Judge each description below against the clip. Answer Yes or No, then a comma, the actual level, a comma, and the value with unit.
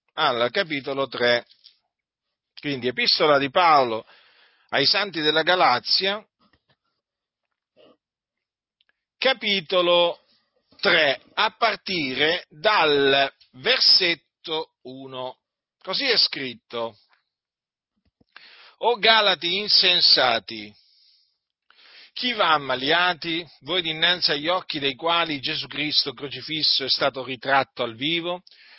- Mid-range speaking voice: Yes, medium, 155 Hz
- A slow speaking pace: Yes, slow, 85 wpm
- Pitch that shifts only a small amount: No, average, 4.9 semitones